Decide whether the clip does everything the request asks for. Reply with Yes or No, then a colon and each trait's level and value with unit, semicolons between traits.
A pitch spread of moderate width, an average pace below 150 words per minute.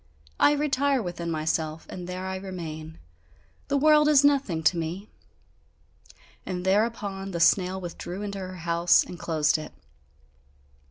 Yes: average, 3.9 semitones; average, 140 wpm